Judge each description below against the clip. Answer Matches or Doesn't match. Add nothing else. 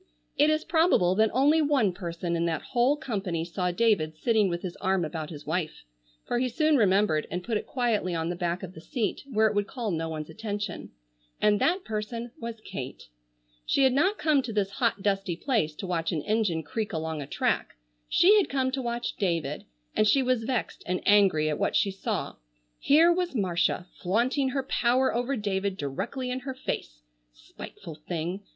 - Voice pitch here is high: Matches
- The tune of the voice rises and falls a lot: Matches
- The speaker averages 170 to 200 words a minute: Matches